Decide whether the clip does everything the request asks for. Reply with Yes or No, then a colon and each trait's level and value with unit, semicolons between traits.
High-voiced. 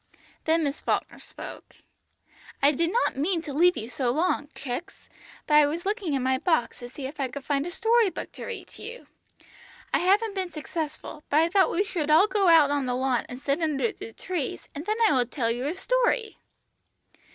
Yes: very high, 310 Hz